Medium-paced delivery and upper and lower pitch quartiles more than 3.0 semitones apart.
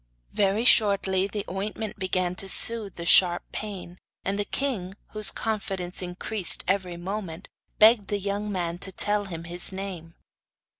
No: average, 150 wpm; narrow, 2.6 semitones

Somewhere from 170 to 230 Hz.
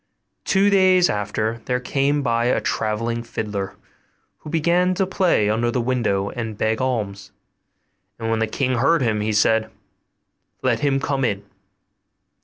No: low, 120 Hz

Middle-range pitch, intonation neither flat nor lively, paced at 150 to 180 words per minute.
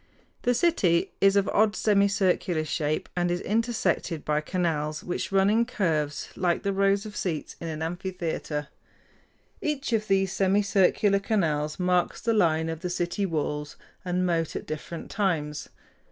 Yes: medium, 180 Hz; average, 3.8 semitones; average, 155 wpm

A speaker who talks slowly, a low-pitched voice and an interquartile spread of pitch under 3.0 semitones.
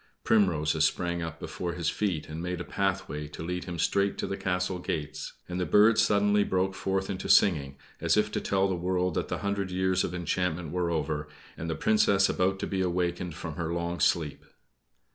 No: average, 200 wpm; very low, 90 Hz; narrow, 2.4 semitones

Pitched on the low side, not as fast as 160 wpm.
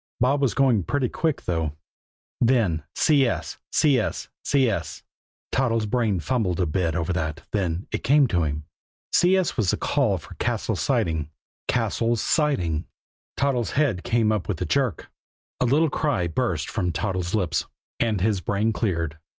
Yes: low, 110 Hz; average, 150 wpm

